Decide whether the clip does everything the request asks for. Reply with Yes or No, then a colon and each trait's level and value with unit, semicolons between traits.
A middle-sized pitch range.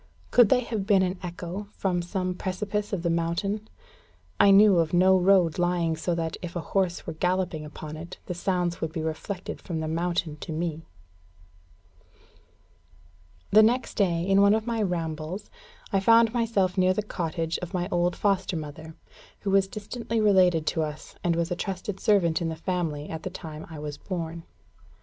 Yes: average, 3.1 semitones